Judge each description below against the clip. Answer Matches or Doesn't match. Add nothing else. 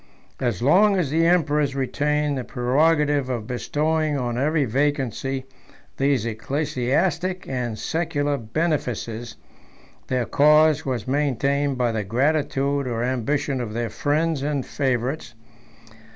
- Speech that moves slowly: Matches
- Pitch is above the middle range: Doesn't match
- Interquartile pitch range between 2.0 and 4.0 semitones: Matches